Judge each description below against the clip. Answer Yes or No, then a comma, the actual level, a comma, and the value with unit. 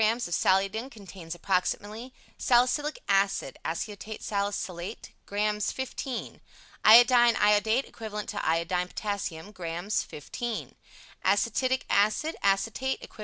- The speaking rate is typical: No, slow, 105 wpm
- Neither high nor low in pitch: No, high, 210 Hz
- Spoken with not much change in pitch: No, average, 3.4 semitones